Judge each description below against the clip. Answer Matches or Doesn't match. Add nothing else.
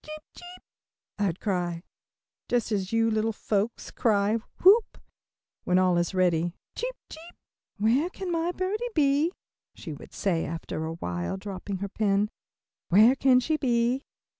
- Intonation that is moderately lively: Doesn't match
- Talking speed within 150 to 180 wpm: Doesn't match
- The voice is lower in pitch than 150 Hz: Doesn't match